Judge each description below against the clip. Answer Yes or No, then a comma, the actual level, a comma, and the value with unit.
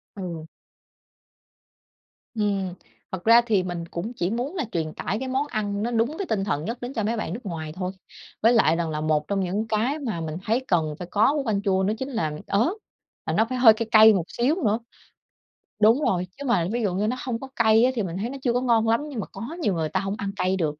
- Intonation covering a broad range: No, average, 4.6 semitones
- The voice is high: Yes, high, 215 Hz